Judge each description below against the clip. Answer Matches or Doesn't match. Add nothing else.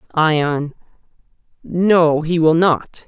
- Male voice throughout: Matches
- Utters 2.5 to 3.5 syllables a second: Matches